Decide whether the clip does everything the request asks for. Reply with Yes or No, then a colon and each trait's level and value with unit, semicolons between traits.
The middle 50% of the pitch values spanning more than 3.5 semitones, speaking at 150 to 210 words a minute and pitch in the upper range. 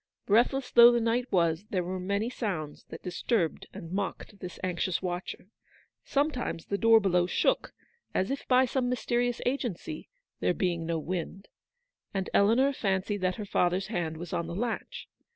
Yes: average, 5.2 semitones; average, 170 wpm; high, 200 Hz